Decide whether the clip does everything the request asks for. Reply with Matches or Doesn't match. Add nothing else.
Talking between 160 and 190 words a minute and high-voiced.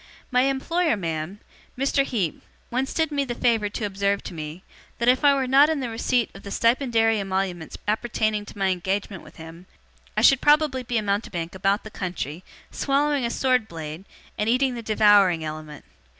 Matches